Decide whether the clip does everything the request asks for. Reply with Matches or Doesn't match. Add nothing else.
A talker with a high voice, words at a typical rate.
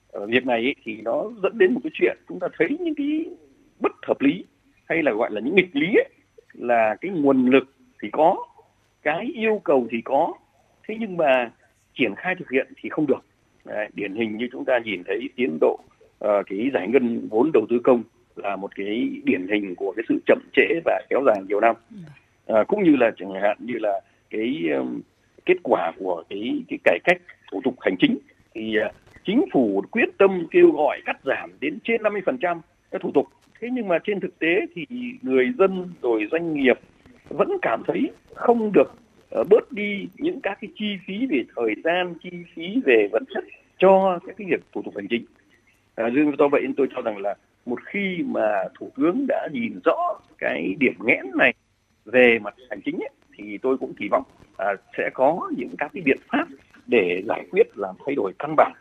Matches